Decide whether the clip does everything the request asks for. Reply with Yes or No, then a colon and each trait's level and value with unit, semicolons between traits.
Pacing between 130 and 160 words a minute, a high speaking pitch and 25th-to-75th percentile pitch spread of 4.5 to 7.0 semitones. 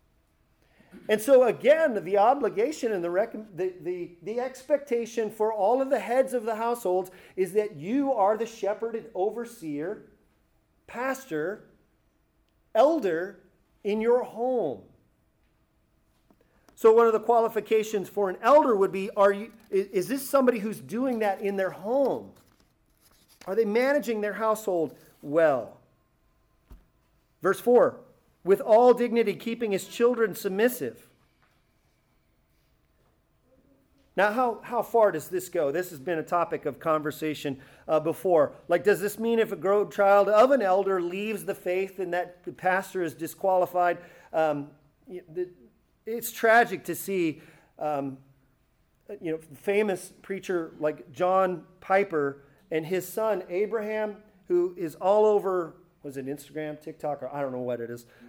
Yes: average, 140 wpm; high, 195 Hz; average, 4.9 semitones